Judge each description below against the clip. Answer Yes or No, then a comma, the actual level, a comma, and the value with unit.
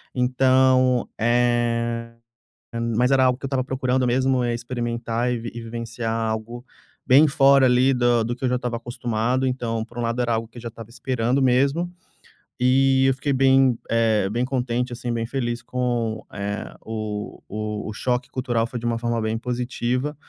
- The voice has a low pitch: Yes, low, 120 Hz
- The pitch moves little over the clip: Yes, narrow, 1.8 semitones